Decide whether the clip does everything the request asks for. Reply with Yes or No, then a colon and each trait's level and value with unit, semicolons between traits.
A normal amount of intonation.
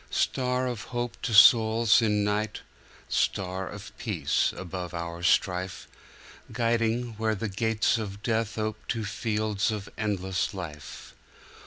Yes: average, 3.1 semitones